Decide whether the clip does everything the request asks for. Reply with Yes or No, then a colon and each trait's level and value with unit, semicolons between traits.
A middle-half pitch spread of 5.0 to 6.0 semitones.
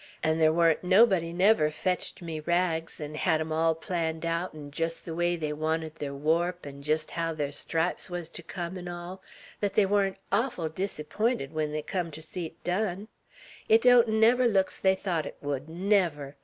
No: average, 3.2 semitones